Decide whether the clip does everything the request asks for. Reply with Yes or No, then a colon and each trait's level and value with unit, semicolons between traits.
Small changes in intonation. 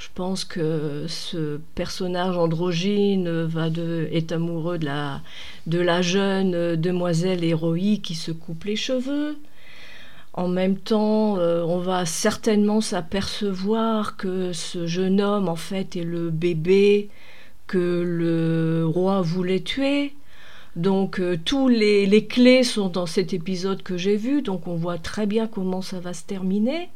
No: average, 3.2 semitones